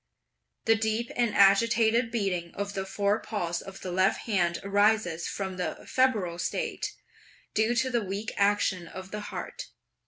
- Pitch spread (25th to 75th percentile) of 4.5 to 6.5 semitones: No, average, 2.9 semitones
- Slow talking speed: No, average, 150 wpm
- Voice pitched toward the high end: Yes, high, 200 Hz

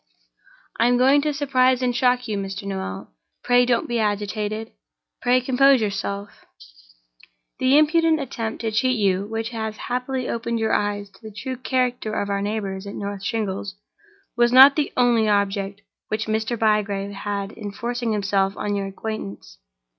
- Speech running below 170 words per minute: Yes, average, 160 wpm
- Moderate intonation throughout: Yes, average, 3.6 semitones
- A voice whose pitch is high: Yes, high, 220 Hz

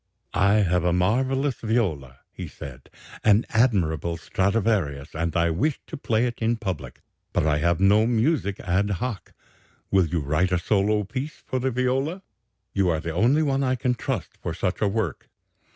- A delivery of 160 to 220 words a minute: Yes, average, 175 wpm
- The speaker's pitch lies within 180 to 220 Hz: No, low, 100 Hz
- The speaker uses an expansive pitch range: Yes, wide, 6.2 semitones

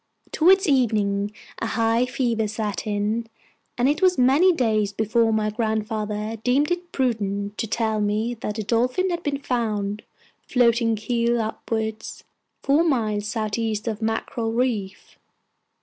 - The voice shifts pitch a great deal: No, average, 2.7 semitones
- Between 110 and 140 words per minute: Yes, slow, 135 wpm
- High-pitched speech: Yes, high, 225 Hz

